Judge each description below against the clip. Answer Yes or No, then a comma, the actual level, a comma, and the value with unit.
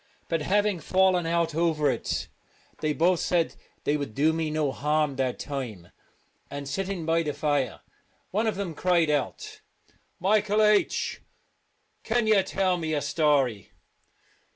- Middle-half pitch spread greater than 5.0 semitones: No, average, 4.3 semitones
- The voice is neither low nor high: Yes, medium, 160 Hz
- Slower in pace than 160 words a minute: Yes, average, 150 wpm